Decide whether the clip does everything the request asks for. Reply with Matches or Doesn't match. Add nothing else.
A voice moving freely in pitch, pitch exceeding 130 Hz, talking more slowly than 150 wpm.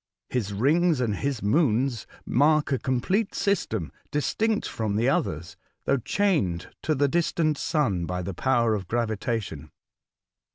Doesn't match